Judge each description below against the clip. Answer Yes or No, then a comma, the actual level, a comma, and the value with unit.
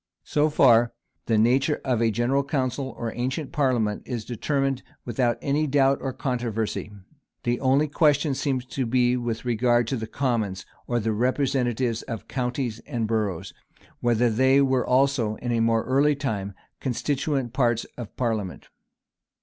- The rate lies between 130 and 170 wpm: Yes, average, 150 wpm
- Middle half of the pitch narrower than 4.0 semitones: Yes, average, 2.9 semitones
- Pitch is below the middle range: Yes, low, 125 Hz